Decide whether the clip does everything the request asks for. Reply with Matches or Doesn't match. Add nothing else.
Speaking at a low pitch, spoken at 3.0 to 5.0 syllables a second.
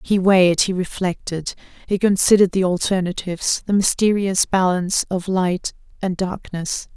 Doesn't match